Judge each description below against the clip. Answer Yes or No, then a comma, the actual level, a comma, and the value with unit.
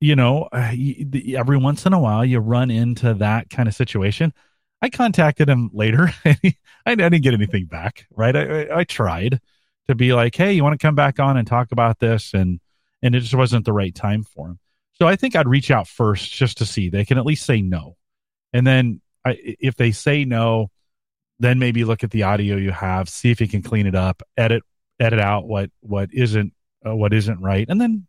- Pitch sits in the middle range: No, low, 120 Hz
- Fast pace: Yes, fast, 220 wpm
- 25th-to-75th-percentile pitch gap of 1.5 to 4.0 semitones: No, average, 4.6 semitones